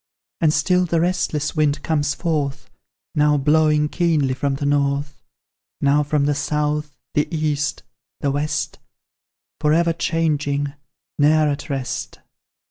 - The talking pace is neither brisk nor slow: No, slow, 125 wpm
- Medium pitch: Yes, medium, 150 Hz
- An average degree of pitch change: No, narrow, 1.6 semitones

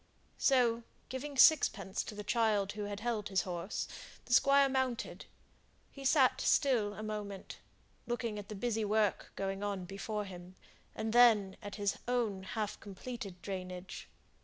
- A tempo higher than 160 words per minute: No, average, 150 wpm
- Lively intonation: No, average, 3.5 semitones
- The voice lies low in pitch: No, high, 210 Hz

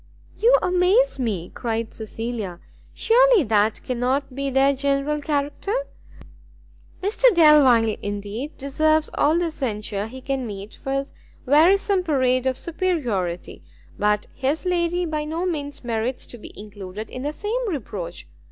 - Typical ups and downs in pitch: No, wide, 6.3 semitones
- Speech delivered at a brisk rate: No, slow, 135 wpm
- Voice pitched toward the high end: Yes, very high, 275 Hz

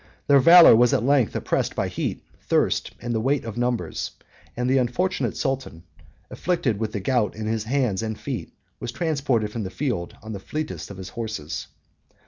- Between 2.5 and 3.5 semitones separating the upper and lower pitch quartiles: No, average, 3.9 semitones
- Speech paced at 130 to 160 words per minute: No, average, 185 wpm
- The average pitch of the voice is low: Yes, low, 120 Hz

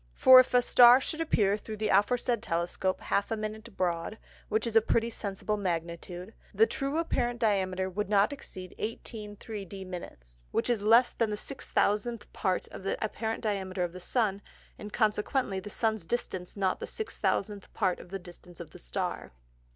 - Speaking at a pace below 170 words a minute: No, average, 180 wpm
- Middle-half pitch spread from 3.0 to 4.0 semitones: Yes, average, 3.5 semitones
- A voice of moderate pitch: No, high, 210 Hz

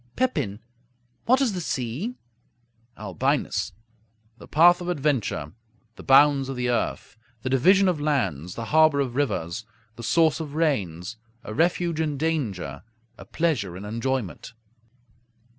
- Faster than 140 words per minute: No, slow, 135 wpm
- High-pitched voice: No, low, 135 Hz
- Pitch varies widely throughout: Yes, wide, 6.9 semitones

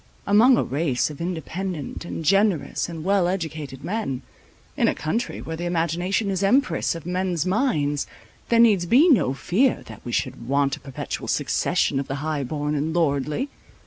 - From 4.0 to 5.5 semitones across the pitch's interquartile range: Yes, average, 5.2 semitones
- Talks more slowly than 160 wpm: No, average, 175 wpm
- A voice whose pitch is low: No, medium, 170 Hz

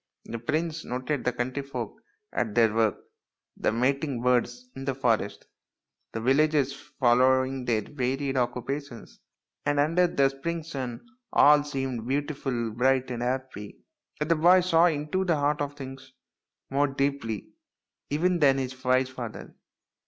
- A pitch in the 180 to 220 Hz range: No, low, 135 Hz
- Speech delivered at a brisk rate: No, average, 145 wpm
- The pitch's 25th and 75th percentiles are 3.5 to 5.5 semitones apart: No, average, 2.9 semitones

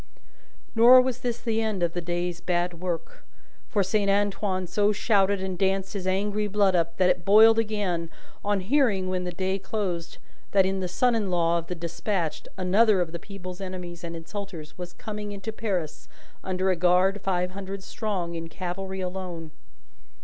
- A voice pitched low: No, high, 190 Hz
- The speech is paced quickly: No, average, 180 wpm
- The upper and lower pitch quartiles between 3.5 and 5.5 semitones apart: No, narrow, 2.6 semitones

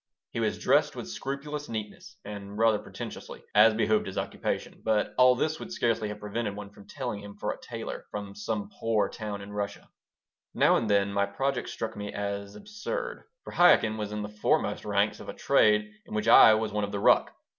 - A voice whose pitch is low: Yes, low, 105 Hz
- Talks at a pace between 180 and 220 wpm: Yes, fast, 205 wpm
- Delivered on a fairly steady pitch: Yes, narrow, 2.0 semitones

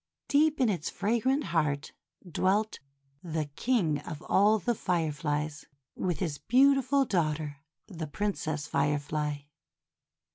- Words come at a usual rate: No, slow, 115 wpm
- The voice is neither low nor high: Yes, medium, 170 Hz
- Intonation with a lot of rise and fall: Yes, wide, 6.6 semitones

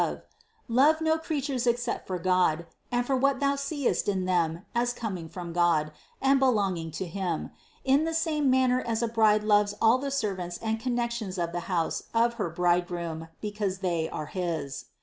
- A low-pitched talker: No, high, 210 Hz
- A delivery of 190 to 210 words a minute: No, average, 180 wpm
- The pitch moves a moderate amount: No, wide, 6.5 semitones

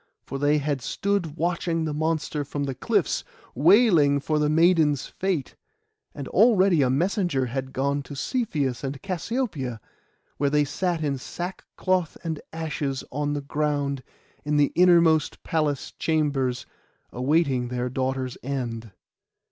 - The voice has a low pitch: No, medium, 150 Hz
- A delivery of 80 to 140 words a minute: Yes, slow, 135 wpm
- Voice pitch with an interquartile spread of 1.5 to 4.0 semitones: Yes, average, 3.5 semitones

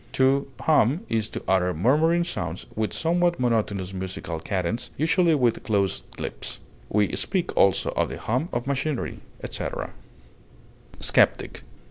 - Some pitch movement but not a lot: No, wide, 8.2 semitones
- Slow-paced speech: Yes, slow, 130 wpm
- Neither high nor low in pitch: No, low, 120 Hz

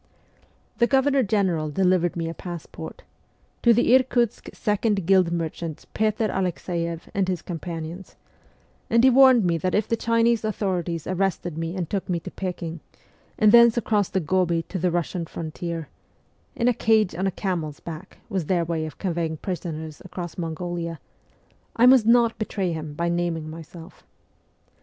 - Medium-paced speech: Yes, average, 160 wpm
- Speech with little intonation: No, average, 4.2 semitones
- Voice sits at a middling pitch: Yes, medium, 180 Hz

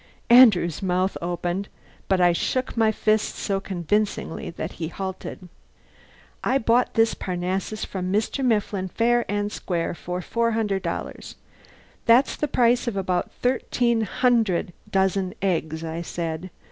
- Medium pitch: No, high, 195 Hz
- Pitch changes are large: No, average, 4.3 semitones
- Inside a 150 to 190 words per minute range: No, slow, 135 wpm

